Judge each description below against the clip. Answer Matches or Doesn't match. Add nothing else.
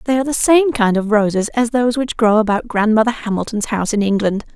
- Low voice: Doesn't match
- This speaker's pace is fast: Matches